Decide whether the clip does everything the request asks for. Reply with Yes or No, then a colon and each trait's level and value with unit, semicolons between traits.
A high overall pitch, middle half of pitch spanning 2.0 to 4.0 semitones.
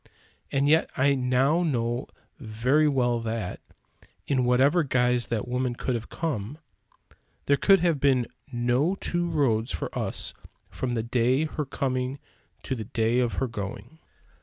No: low, 125 Hz; average, 3.0 semitones